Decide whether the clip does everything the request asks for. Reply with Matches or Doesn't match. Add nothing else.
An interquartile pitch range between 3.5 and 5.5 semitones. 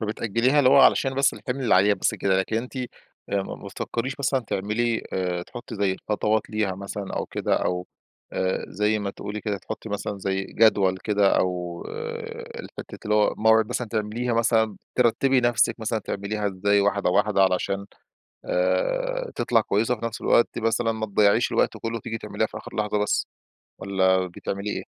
Doesn't match